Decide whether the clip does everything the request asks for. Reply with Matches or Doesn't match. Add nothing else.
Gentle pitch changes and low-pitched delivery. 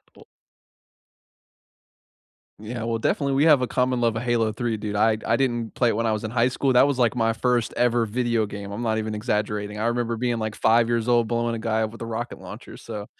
Matches